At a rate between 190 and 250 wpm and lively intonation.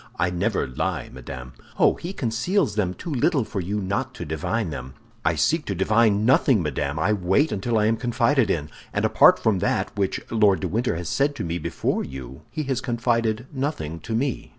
Yes: average, 200 wpm; wide, 5.8 semitones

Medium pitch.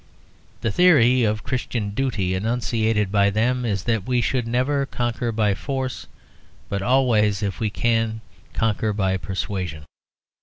No: low, 110 Hz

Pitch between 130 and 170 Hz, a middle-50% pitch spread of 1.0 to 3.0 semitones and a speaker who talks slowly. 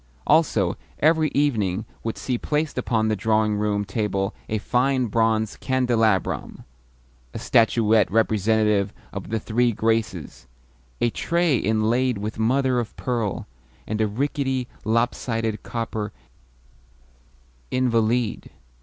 No: low, 115 Hz; average, 2.7 semitones; slow, 115 wpm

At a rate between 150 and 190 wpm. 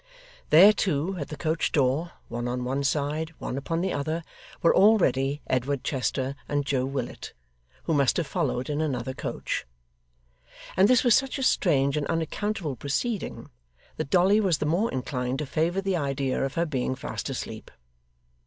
Yes: average, 170 wpm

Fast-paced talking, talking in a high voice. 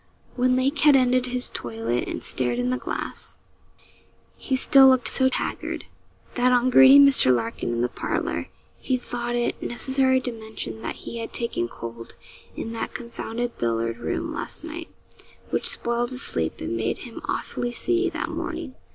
No: average, 170 wpm; high, 240 Hz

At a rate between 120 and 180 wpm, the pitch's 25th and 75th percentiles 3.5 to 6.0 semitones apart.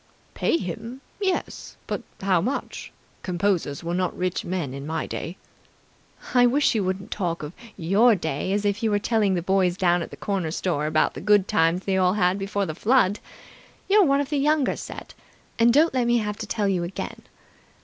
No: average, 195 wpm; average, 4.6 semitones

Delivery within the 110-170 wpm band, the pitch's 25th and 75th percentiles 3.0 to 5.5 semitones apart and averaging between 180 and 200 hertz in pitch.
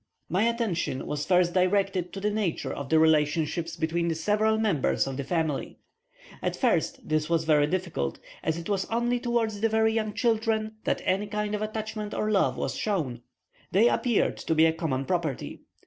No: average, 185 wpm; average, 5.2 semitones; medium, 185 Hz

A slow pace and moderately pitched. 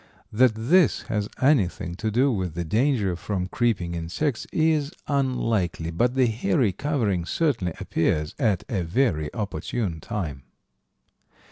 No: slow, 130 wpm; low, 110 Hz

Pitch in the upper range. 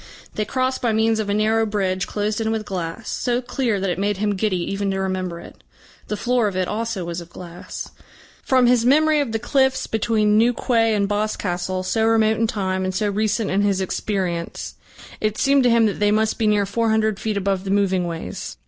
Yes: high, 210 Hz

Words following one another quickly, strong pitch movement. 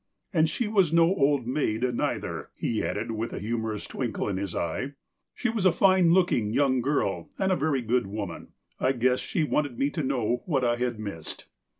Yes: fast, 210 wpm; wide, 6.1 semitones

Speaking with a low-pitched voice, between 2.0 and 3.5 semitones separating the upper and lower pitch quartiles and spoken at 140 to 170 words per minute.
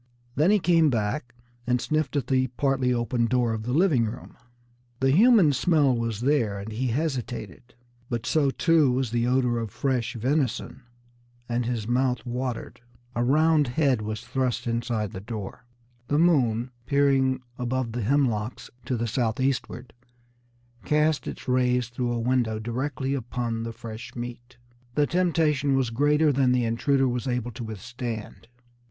Yes: low, 125 Hz; average, 3.0 semitones; average, 155 wpm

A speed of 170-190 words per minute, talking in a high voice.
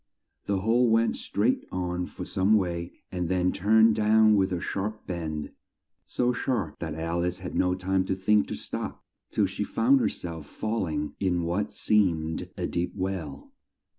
No: average, 175 wpm; very low, 95 Hz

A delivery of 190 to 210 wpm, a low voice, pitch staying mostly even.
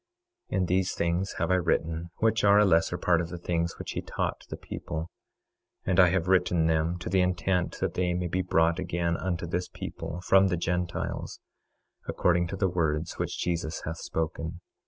Yes: average, 195 wpm; very low, 85 Hz; narrow, 1.7 semitones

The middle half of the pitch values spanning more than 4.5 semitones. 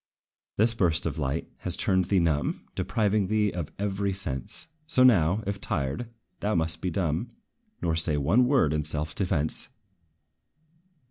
Yes: average, 4.9 semitones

